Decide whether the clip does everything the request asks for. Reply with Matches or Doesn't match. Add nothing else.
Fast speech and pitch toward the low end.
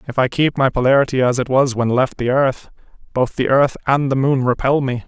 Matches